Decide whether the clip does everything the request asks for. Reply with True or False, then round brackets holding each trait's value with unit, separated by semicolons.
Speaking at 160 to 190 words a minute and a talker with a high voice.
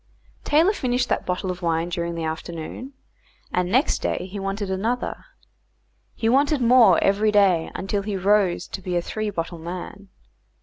True (165 wpm; 195 Hz)